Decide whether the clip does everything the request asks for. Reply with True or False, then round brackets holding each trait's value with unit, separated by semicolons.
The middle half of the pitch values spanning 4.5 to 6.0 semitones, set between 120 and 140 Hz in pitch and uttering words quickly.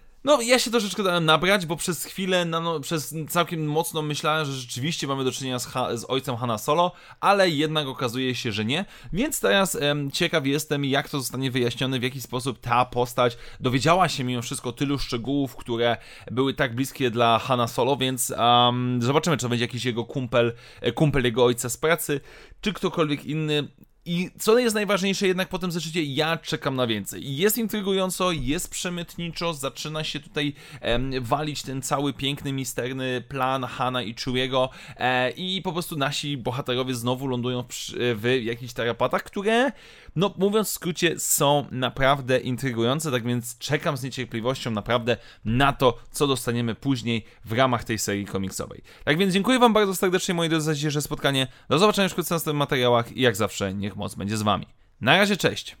True (5.0 semitones; 135 Hz; 185 wpm)